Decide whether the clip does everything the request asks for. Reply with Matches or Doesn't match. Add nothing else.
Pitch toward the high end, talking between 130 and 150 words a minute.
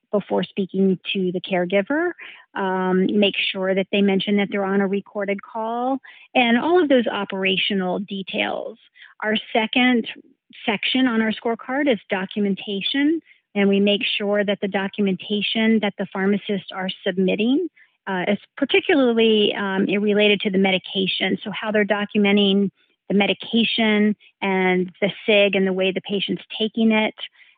Matches